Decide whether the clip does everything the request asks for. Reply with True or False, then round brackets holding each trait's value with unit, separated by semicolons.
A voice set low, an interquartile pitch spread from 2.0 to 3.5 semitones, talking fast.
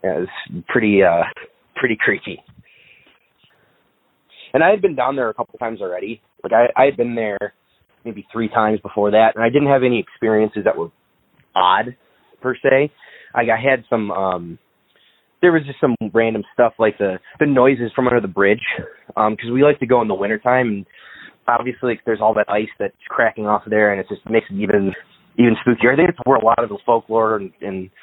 True (115 Hz; 3.1 semitones; 210 wpm)